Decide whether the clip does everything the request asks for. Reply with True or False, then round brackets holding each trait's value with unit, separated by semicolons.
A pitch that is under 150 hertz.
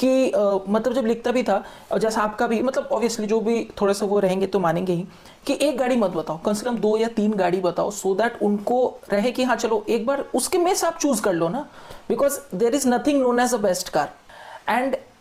False (230 Hz)